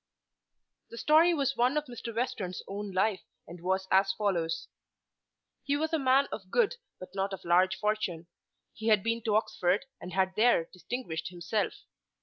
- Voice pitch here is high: Yes, high, 210 Hz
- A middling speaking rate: Yes, average, 165 wpm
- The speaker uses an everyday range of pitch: Yes, average, 5.0 semitones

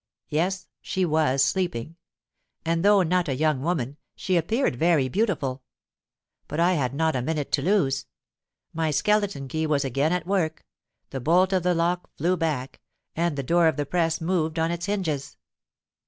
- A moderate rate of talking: Yes, average, 160 wpm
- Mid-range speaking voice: Yes, medium, 160 Hz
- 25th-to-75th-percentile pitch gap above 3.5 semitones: Yes, average, 4.0 semitones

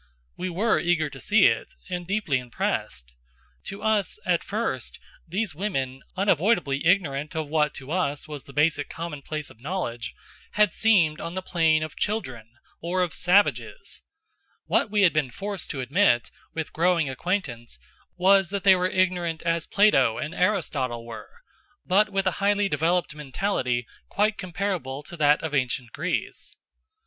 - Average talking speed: Yes, average, 155 wpm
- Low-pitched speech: No, medium, 170 Hz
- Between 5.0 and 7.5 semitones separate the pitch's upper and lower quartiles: Yes, wide, 5.4 semitones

